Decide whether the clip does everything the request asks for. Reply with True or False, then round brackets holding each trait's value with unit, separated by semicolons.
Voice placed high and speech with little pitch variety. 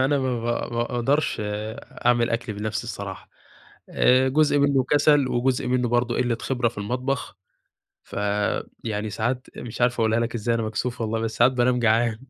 False (120 Hz; 2.3 semitones)